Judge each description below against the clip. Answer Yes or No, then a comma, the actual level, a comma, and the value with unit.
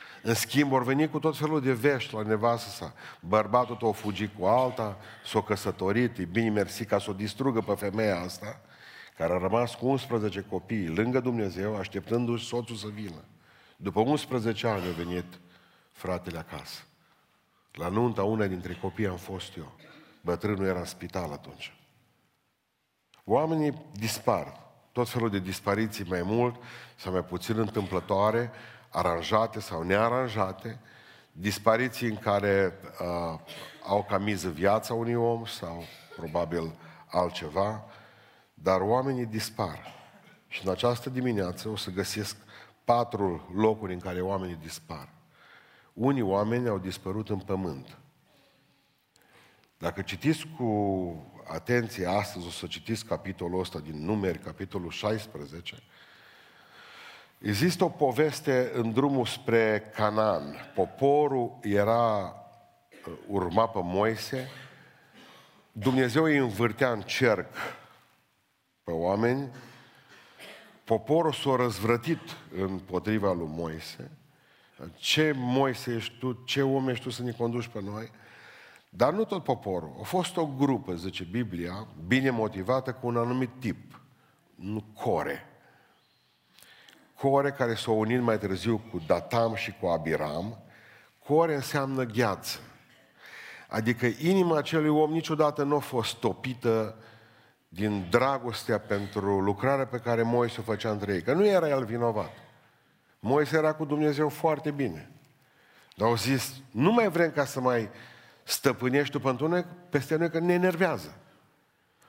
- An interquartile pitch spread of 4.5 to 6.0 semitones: Yes, average, 4.8 semitones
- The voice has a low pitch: Yes, low, 115 Hz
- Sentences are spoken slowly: No, average, 130 wpm